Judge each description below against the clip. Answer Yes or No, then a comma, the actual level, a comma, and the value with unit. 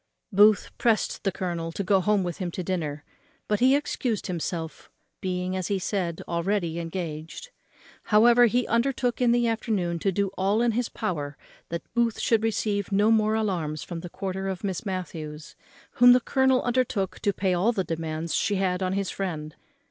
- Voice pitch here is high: Yes, high, 195 Hz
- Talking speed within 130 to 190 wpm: Yes, average, 180 wpm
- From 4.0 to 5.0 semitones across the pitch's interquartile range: Yes, average, 4.3 semitones